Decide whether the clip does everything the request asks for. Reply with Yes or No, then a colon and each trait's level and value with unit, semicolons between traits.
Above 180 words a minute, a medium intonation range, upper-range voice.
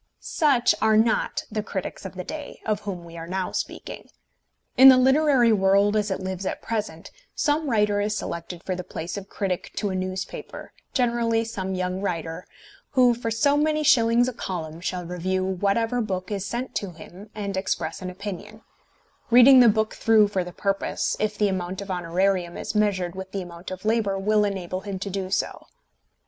Yes: average, 190 wpm; average, 3.4 semitones; high, 200 Hz